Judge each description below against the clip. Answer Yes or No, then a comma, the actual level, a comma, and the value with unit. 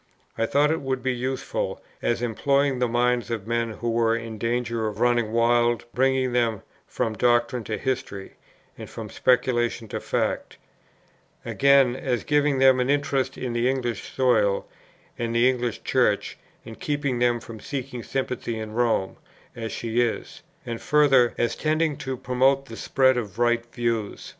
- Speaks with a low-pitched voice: Yes, low, 120 Hz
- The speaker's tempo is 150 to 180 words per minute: Yes, average, 160 wpm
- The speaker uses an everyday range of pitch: No, narrow, 2.2 semitones